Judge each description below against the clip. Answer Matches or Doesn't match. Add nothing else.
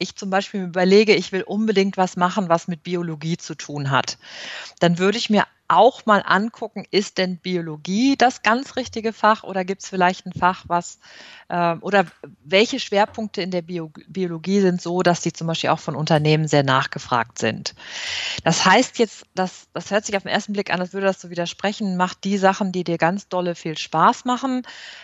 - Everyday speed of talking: Doesn't match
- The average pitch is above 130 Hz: Matches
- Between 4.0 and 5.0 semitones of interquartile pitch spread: Doesn't match